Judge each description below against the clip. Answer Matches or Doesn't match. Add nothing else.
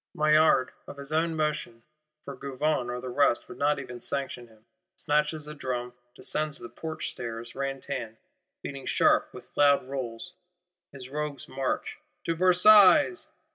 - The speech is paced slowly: Doesn't match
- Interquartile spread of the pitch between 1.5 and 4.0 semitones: Matches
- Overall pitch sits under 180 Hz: Matches